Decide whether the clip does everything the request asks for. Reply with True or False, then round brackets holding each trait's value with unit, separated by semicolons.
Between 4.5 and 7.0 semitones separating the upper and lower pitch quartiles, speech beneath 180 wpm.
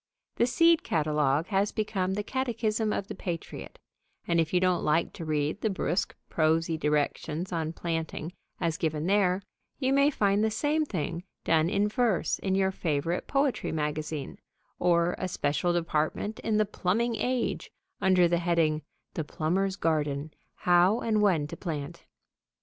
True (4.8 semitones; 155 wpm)